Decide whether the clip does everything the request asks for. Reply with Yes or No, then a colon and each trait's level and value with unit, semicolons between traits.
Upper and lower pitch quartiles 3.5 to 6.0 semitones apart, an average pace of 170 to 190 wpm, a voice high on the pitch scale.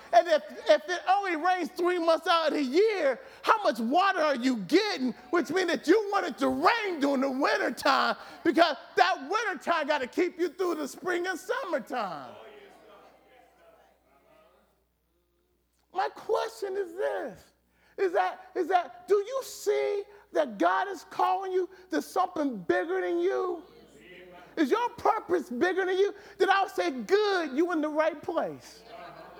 No: average, 3.8 semitones; average, 155 wpm; very high, 360 Hz